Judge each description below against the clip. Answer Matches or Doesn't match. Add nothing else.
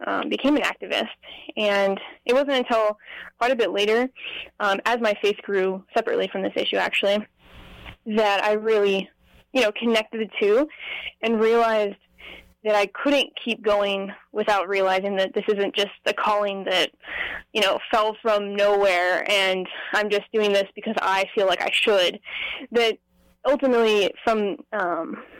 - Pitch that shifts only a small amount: Matches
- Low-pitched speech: Doesn't match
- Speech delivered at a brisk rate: Doesn't match